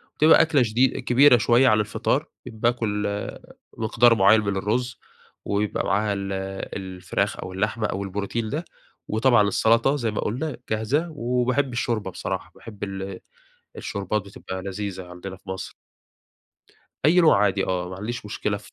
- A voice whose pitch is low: Yes, low, 105 Hz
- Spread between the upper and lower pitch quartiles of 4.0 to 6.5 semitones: No, average, 3.6 semitones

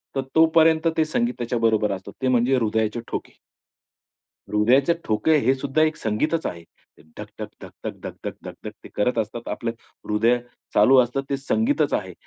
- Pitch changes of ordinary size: No, wide, 6.1 semitones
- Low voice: Yes, low, 125 Hz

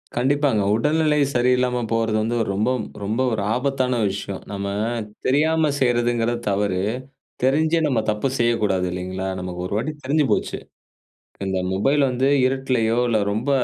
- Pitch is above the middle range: No, low, 120 Hz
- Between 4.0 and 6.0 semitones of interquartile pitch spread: Yes, average, 4.4 semitones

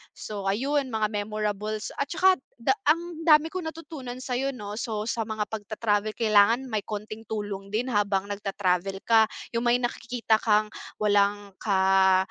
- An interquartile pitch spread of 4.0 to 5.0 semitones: No, average, 3.2 semitones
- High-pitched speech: Yes, high, 215 Hz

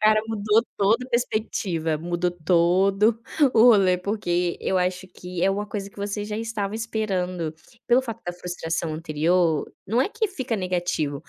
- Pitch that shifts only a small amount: No, average, 3.6 semitones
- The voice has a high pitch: Yes, high, 195 Hz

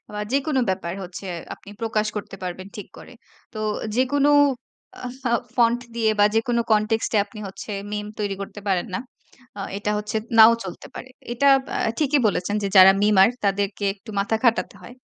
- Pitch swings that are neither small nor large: Yes, average, 3.1 semitones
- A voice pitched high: Yes, high, 210 Hz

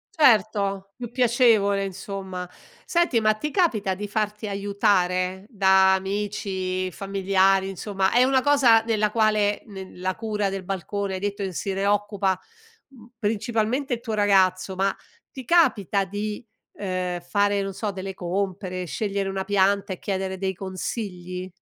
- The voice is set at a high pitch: Yes, high, 200 Hz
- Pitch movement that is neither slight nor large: No, narrow, 2.1 semitones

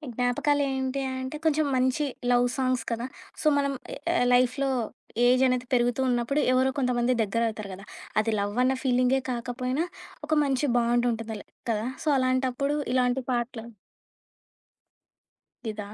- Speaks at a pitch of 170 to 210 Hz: No, very high, 250 Hz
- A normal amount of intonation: No, narrow, 1.8 semitones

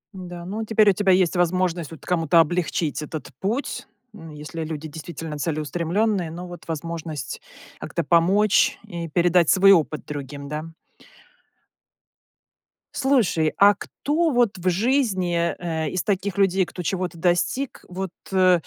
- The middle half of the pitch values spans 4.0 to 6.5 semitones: No, average, 3.2 semitones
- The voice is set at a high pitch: No, medium, 175 Hz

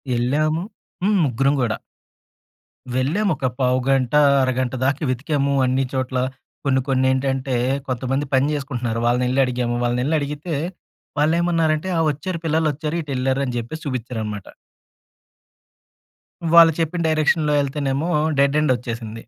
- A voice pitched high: No, low, 135 Hz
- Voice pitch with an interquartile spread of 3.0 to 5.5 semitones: Yes, average, 3.3 semitones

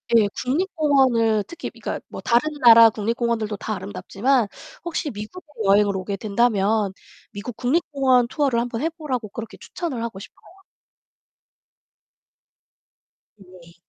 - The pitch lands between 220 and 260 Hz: Yes, high, 230 Hz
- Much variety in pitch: No, average, 4.3 semitones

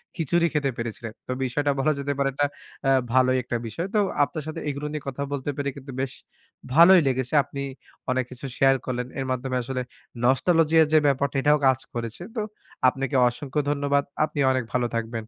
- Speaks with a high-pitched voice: No, low, 135 Hz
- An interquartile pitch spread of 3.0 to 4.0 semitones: No, narrow, 2.5 semitones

